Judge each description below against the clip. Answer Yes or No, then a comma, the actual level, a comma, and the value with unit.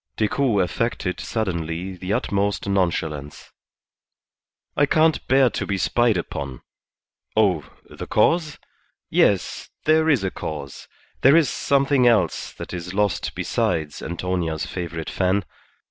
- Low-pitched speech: Yes, very low, 95 Hz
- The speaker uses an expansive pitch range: Yes, wide, 6.1 semitones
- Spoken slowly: Yes, slow, 120 wpm